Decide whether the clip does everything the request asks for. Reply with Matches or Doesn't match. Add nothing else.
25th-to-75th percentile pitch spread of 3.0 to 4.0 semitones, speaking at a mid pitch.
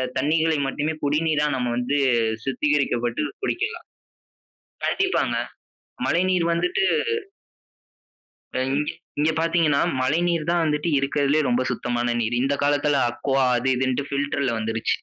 Matches